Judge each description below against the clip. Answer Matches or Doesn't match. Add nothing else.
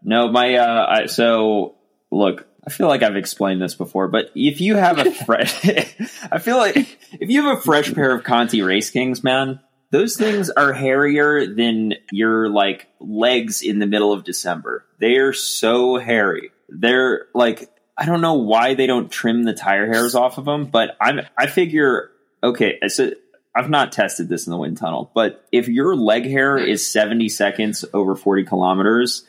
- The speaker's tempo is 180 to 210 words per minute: Matches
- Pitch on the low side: Matches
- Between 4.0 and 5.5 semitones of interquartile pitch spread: Matches